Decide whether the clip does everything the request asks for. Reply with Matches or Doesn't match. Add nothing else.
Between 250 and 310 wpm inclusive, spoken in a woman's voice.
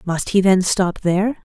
Doesn't match